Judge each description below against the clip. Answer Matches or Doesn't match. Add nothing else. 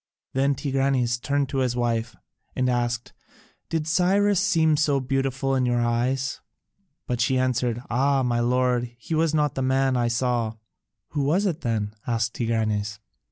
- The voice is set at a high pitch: Doesn't match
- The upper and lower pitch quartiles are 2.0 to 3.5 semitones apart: Matches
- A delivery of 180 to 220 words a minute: Doesn't match